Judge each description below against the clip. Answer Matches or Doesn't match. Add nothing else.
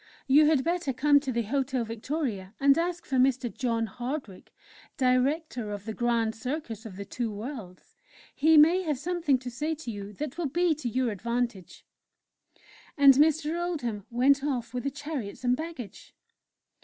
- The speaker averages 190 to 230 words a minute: Doesn't match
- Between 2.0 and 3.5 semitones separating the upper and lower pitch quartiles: Doesn't match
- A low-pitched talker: Doesn't match